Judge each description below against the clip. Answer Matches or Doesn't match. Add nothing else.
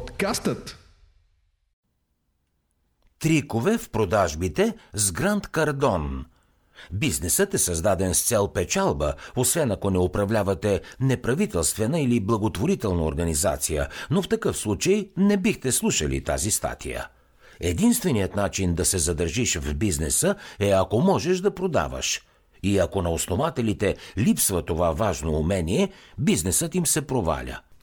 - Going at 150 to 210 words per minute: Doesn't match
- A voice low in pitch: Matches